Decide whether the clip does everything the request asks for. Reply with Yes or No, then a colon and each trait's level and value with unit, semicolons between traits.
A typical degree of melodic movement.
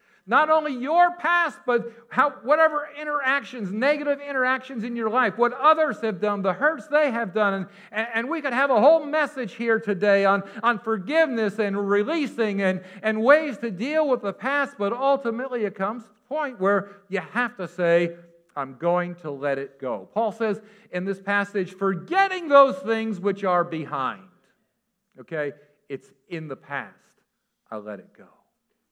No: wide, 6.0 semitones